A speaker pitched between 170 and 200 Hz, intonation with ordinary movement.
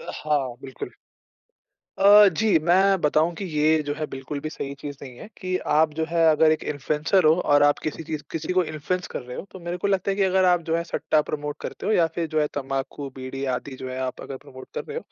No: medium, 155 Hz; average, 3.9 semitones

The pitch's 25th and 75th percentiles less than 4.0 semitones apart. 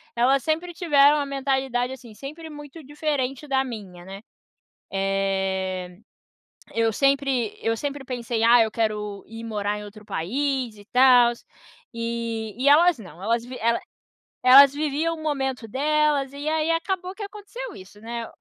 No: average, 4.7 semitones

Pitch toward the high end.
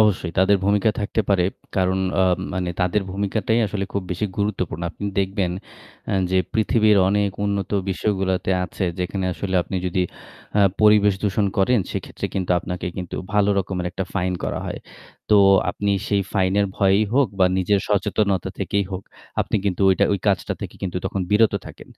No: low, 100 Hz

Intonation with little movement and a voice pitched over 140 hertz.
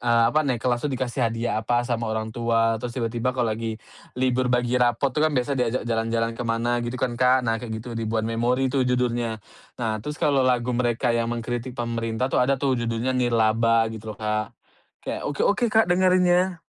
No: narrow, 1.9 semitones; low, 120 Hz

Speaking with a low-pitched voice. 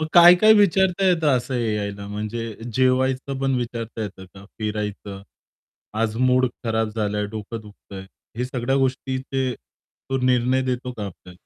Yes: low, 120 Hz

